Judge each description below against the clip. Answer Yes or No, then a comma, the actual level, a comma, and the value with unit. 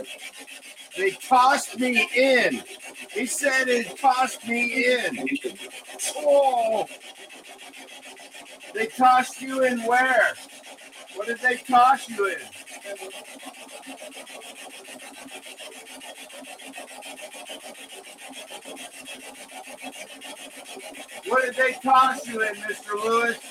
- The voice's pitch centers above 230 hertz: Yes, very high, 255 Hz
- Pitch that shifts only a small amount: Yes, narrow, 2.0 semitones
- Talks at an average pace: No, slow, 75 wpm